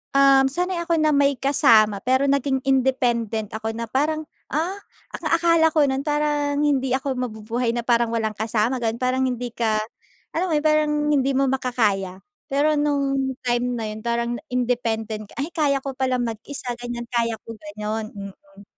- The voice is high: Yes, very high, 255 Hz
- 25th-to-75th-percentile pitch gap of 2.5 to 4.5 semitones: Yes, average, 3.6 semitones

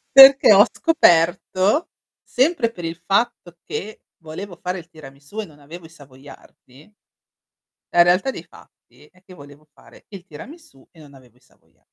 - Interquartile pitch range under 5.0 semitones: No, wide, 5.5 semitones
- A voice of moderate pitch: Yes, medium, 175 Hz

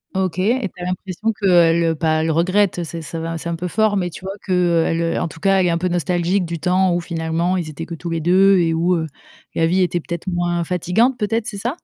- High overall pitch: No, medium, 175 Hz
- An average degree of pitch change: No, narrow, 2.2 semitones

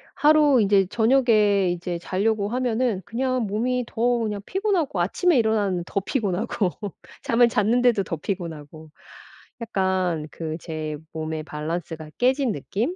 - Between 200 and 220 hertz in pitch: Yes, high, 205 Hz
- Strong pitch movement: Yes, wide, 5.8 semitones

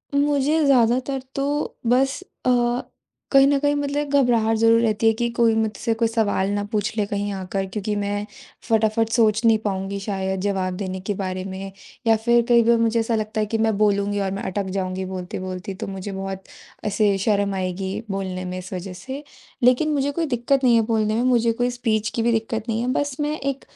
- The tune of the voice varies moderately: Yes, average, 3.5 semitones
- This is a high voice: Yes, high, 220 Hz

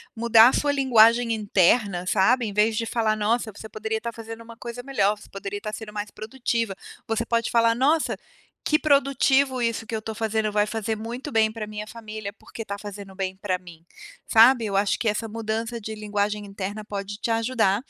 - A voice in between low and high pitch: No, high, 220 Hz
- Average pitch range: No, narrow, 2.0 semitones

